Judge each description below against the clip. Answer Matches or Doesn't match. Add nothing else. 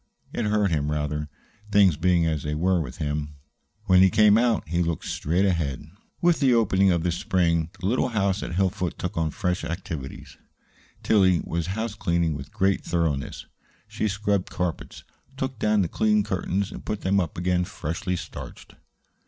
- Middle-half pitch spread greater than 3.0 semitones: Matches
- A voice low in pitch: Matches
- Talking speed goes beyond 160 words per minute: Matches